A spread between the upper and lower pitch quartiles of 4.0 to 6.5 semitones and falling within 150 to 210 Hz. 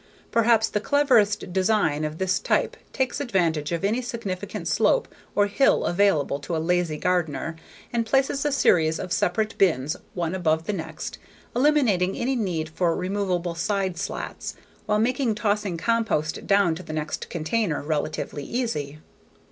Yes: wide, 5.6 semitones; high, 190 Hz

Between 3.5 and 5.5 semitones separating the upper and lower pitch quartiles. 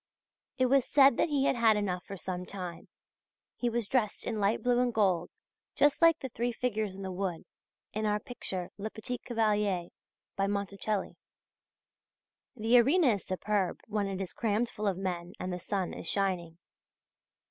Yes: average, 4.1 semitones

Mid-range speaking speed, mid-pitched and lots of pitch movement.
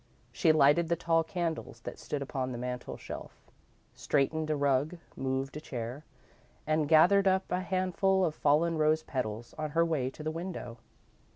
No: average, 170 wpm; medium, 155 Hz; average, 3.8 semitones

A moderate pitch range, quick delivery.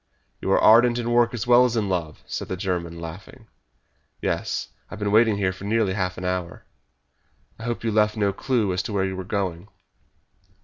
Yes: average, 3.7 semitones; fast, 210 wpm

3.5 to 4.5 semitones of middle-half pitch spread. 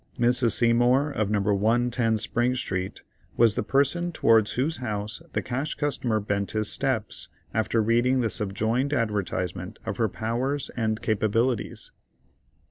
No: average, 2.9 semitones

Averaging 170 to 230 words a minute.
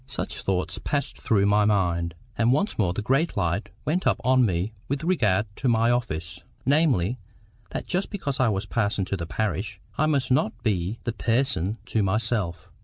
Yes: average, 180 wpm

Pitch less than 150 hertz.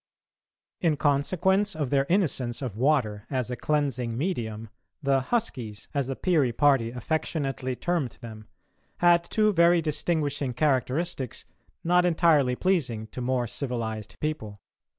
Yes: medium, 140 Hz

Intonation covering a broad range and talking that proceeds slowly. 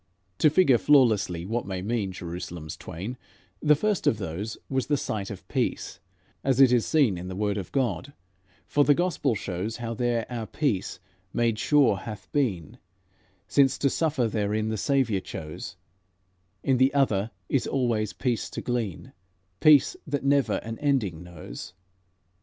No: wide, 5.7 semitones; average, 160 wpm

